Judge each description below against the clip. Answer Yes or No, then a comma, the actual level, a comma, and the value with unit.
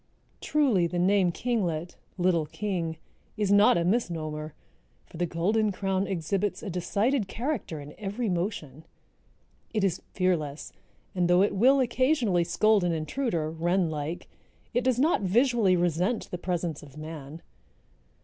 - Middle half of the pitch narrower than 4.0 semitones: No, average, 4.5 semitones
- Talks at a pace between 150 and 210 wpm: No, slow, 135 wpm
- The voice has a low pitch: No, medium, 185 Hz